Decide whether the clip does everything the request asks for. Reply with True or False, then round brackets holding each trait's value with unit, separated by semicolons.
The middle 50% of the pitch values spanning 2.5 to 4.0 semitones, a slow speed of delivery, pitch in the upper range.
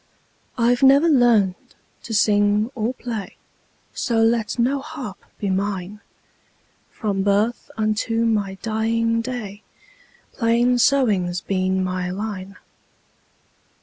True (3.2 semitones; 100 wpm; 220 Hz)